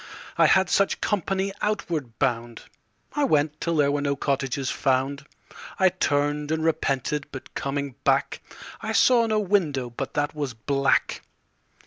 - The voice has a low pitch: No, medium, 145 Hz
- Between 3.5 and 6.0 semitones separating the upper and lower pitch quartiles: Yes, average, 4.3 semitones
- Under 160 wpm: Yes, average, 145 wpm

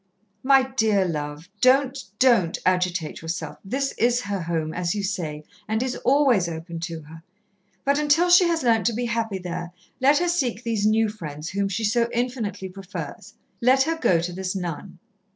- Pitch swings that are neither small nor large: No, wide, 6.6 semitones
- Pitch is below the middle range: No, high, 210 Hz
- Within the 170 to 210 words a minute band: Yes, average, 180 wpm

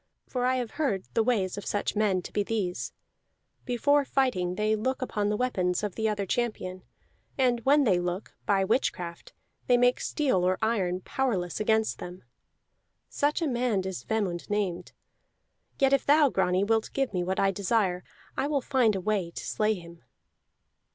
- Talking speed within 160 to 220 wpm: Yes, average, 175 wpm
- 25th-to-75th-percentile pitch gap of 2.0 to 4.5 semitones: No, average, 5.1 semitones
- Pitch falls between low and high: No, high, 210 Hz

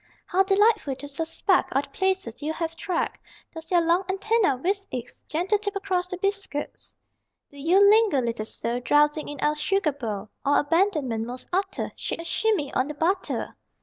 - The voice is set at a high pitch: Yes, very high, 330 Hz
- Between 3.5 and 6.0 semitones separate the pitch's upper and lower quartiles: Yes, wide, 5.4 semitones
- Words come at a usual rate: Yes, average, 180 wpm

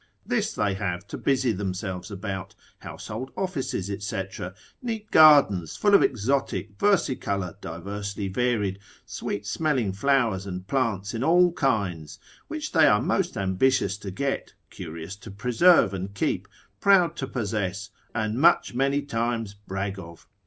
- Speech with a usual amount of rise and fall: No, wide, 5.9 semitones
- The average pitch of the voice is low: Yes, low, 105 Hz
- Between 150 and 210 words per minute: No, average, 140 wpm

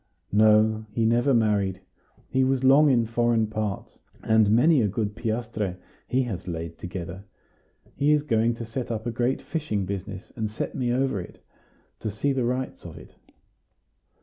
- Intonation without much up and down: No, average, 3.2 semitones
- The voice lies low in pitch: Yes, low, 110 Hz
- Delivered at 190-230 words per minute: No, average, 170 wpm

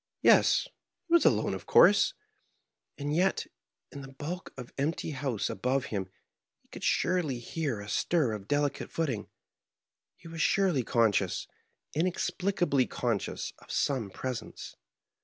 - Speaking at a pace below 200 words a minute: Yes, average, 140 wpm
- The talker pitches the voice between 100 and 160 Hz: Yes, medium, 140 Hz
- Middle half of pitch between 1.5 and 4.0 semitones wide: No, wide, 5.5 semitones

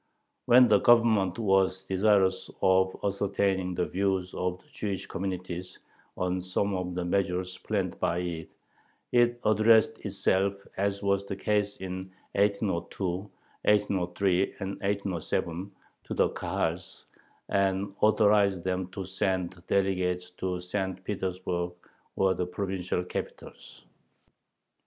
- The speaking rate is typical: No, slow, 120 wpm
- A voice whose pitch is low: Yes, very low, 95 Hz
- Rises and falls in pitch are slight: Yes, narrow, 1.7 semitones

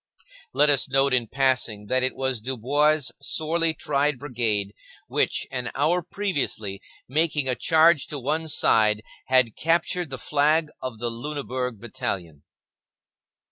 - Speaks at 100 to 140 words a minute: Yes, slow, 135 wpm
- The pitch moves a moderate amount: Yes, average, 4.1 semitones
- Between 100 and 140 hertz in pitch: Yes, low, 135 Hz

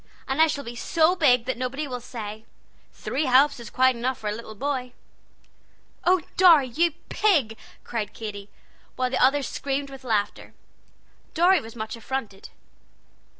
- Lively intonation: No, average, 4.0 semitones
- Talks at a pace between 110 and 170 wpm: Yes, average, 160 wpm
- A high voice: Yes, very high, 255 Hz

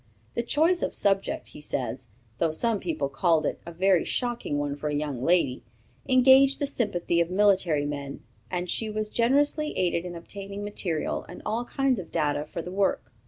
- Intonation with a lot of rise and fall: Yes, wide, 7.0 semitones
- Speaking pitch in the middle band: Yes, medium, 180 Hz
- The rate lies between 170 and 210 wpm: Yes, average, 190 wpm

